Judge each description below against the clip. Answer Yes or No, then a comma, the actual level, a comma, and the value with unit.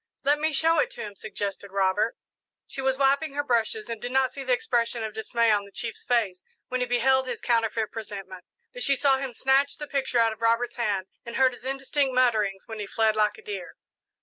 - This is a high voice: Yes, high, 240 Hz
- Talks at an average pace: No, fast, 225 wpm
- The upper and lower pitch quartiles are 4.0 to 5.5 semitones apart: No, average, 3.6 semitones